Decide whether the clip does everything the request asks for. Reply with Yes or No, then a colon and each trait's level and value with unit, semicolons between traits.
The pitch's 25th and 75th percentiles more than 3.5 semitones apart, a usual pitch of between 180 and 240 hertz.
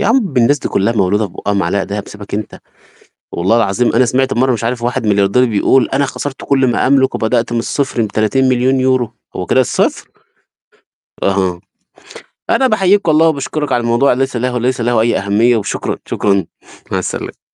No: average, 4.1 semitones; low, 120 Hz